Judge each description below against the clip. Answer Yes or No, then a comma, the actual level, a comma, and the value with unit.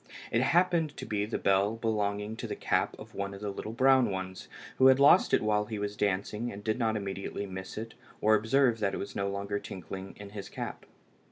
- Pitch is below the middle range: Yes, low, 105 Hz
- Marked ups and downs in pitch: No, narrow, 2.4 semitones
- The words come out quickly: Yes, fast, 225 wpm